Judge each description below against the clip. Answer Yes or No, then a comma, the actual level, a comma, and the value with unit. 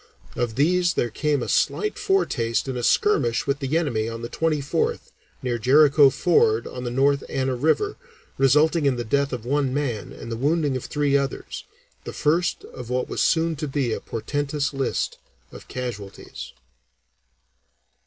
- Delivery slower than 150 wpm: No, average, 165 wpm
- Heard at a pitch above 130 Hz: Yes, medium, 140 Hz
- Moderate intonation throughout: Yes, average, 3.7 semitones